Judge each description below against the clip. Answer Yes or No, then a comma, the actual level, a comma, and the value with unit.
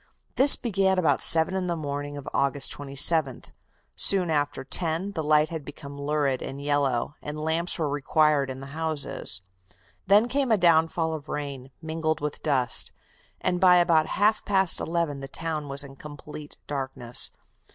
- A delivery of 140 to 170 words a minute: Yes, average, 160 wpm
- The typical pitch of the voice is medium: Yes, medium, 155 Hz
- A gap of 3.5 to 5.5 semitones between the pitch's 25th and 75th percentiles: No, average, 3.0 semitones